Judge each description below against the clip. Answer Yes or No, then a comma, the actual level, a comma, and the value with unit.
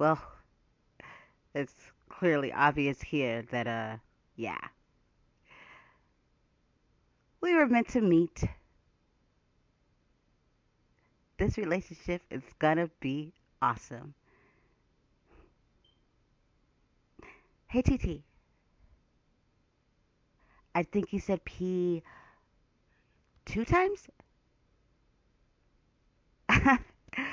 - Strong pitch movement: Yes, wide, 6.2 semitones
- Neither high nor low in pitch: Yes, medium, 155 Hz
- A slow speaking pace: Yes, slow, 60 wpm